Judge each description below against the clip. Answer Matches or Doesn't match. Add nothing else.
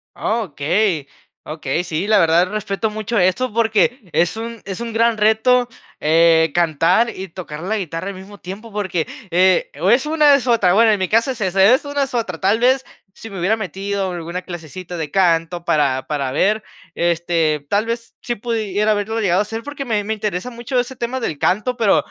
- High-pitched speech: Matches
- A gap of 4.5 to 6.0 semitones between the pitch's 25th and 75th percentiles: Matches